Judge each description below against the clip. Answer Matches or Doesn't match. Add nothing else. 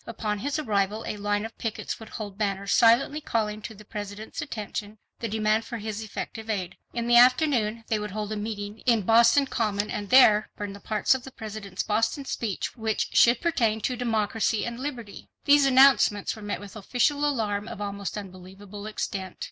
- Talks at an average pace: Matches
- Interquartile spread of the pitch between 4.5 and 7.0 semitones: Doesn't match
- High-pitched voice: Matches